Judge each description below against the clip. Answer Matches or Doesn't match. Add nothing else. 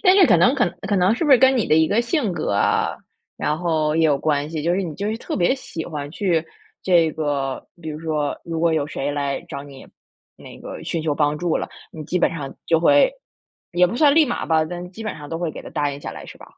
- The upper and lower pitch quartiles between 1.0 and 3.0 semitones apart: Doesn't match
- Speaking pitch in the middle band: Matches